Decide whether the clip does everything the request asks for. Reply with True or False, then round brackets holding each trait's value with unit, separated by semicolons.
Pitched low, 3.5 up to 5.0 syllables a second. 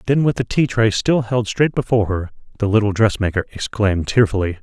False (110 Hz; 5.9 syllables/s)